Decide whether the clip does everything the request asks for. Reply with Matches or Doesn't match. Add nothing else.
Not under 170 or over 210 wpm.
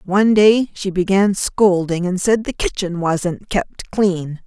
Doesn't match